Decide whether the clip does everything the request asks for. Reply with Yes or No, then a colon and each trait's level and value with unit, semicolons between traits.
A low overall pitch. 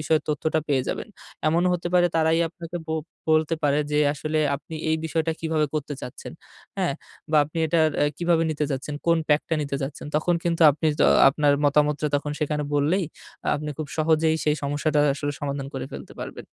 No: medium, 155 Hz